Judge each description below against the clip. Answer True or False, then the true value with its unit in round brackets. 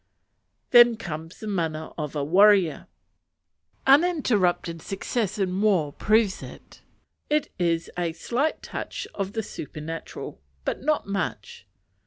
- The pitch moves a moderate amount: False (5.9 semitones)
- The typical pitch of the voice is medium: False (195 Hz)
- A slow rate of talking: True (120 wpm)